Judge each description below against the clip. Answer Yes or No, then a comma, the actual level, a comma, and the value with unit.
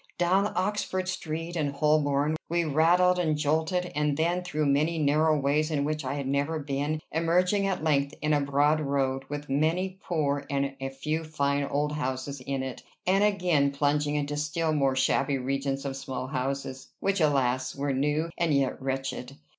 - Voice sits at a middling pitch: Yes, medium, 150 Hz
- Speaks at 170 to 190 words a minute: Yes, average, 175 wpm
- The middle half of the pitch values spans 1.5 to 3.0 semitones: Yes, narrow, 2.6 semitones